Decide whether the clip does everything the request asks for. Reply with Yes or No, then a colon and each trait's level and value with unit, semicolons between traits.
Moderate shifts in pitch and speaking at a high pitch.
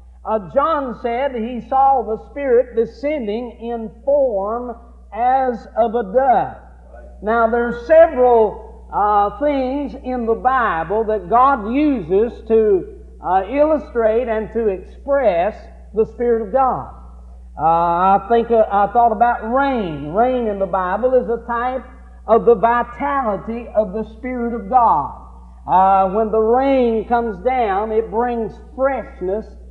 Yes: average, 3.3 semitones; high, 235 Hz